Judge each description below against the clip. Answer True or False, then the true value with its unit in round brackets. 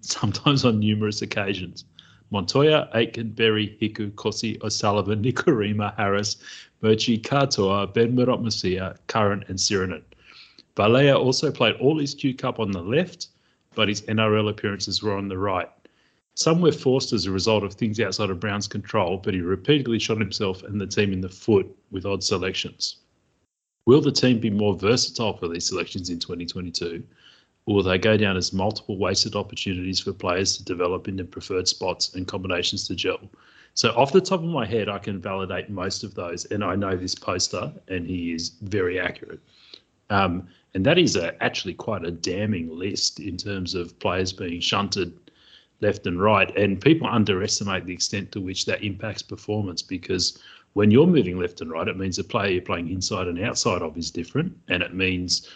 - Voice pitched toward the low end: True (100 Hz)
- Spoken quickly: False (185 wpm)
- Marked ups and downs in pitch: False (3.0 semitones)